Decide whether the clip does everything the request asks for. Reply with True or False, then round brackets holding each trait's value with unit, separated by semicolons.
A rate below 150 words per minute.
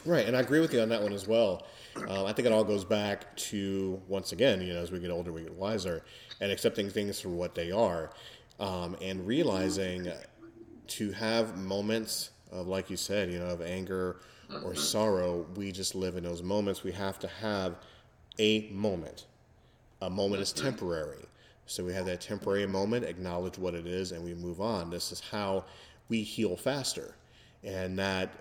False (190 wpm)